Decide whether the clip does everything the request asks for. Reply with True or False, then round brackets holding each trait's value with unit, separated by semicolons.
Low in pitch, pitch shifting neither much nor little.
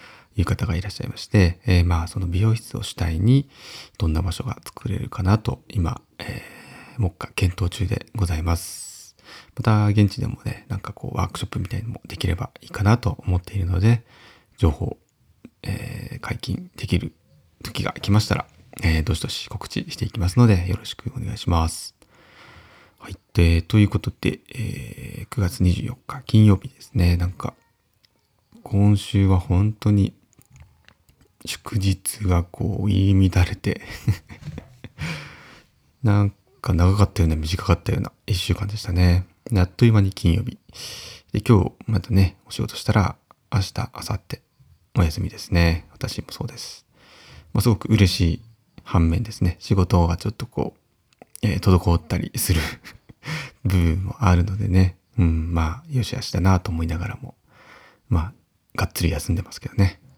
True (100 Hz; 4.0 semitones)